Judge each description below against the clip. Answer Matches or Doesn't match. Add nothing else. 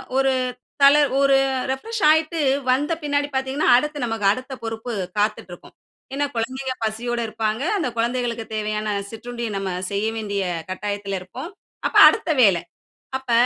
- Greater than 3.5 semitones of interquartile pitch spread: Matches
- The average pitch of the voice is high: Matches